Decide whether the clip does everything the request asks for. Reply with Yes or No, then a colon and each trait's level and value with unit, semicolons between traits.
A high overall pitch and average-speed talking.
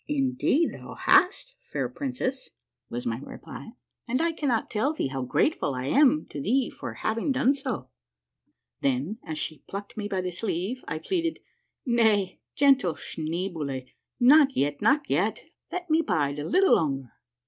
Yes: high, 220 Hz; average, 165 wpm